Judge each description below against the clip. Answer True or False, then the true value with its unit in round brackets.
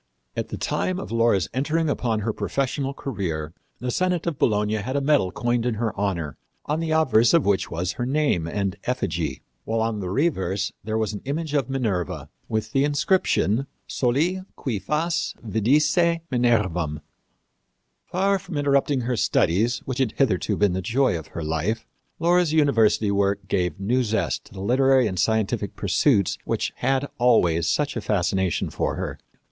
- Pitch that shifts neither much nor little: False (6.1 semitones)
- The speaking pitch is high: False (115 Hz)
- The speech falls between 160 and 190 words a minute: True (170 wpm)